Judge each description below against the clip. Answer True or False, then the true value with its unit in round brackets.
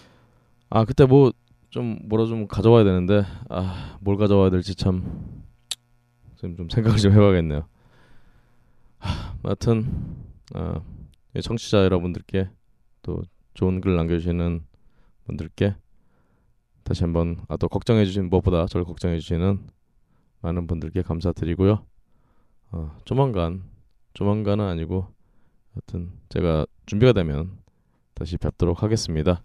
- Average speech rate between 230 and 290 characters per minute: True (255 characters per minute)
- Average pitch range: True (4.5 semitones)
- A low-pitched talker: True (95 Hz)